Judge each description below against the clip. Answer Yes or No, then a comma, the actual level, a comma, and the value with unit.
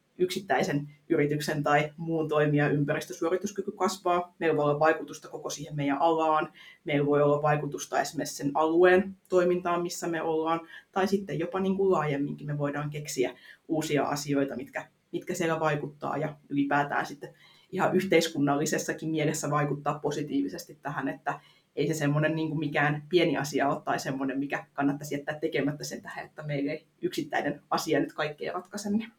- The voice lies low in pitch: No, medium, 155 Hz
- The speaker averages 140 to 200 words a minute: Yes, fast, 155 wpm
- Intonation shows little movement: No, average, 3.2 semitones